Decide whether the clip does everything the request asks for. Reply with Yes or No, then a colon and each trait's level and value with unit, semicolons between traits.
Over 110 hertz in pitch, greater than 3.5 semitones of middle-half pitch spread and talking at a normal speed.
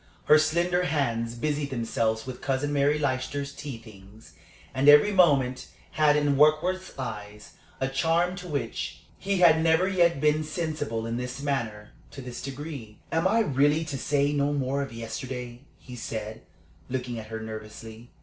Yes: medium, 140 Hz; average, 4.7 semitones; average, 160 wpm